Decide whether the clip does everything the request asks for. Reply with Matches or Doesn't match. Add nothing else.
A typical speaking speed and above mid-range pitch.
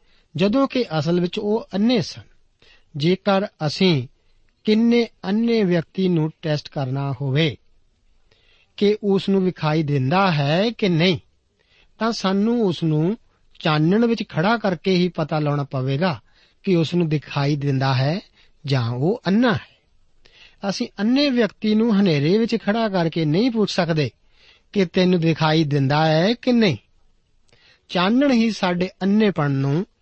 Doesn't match